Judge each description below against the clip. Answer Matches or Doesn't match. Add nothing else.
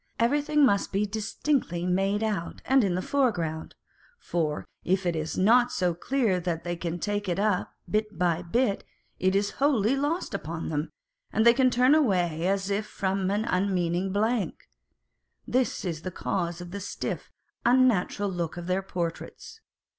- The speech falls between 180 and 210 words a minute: Doesn't match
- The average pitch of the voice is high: Matches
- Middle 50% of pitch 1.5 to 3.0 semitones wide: Doesn't match